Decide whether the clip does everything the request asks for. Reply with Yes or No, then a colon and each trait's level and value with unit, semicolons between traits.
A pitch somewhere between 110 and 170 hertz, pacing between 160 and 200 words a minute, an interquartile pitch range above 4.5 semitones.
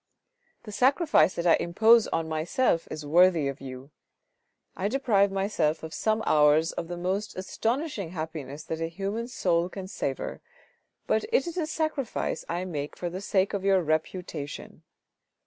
No: medium, 185 Hz; average, 165 wpm; wide, 5.4 semitones